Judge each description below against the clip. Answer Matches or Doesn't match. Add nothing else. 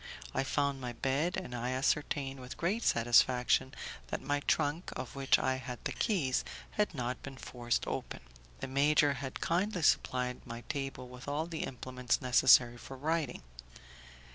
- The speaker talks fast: Doesn't match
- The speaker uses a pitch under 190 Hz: Matches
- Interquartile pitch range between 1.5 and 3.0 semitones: Matches